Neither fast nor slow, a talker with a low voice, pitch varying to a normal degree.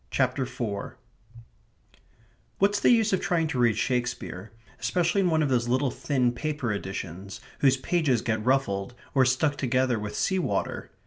Yes: average, 155 wpm; low, 130 Hz; average, 4.9 semitones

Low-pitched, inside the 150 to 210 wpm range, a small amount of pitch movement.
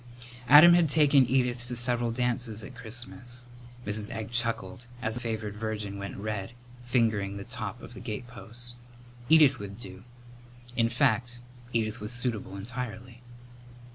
No: low, 120 Hz; average, 140 wpm; narrow, 2.3 semitones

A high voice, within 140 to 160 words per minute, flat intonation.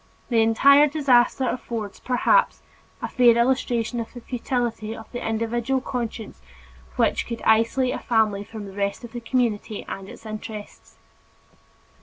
Yes: high, 230 Hz; average, 145 wpm; narrow, 2.1 semitones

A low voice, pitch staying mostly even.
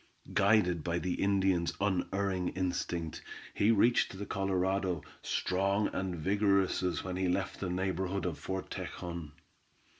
Yes: very low, 95 Hz; narrow, 1.7 semitones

